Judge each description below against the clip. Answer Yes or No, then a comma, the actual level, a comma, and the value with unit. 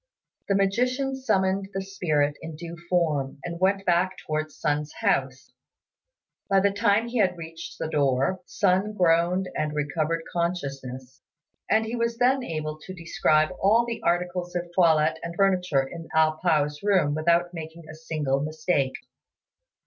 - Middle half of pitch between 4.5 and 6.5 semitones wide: No, average, 3.9 semitones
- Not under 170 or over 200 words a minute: No, average, 150 wpm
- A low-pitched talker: No, medium, 170 Hz